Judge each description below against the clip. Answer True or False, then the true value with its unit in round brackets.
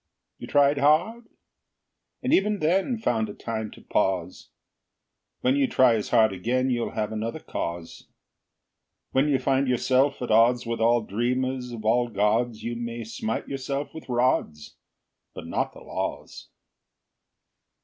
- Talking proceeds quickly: False (145 wpm)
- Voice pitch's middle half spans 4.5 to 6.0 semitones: False (3.6 semitones)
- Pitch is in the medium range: False (120 Hz)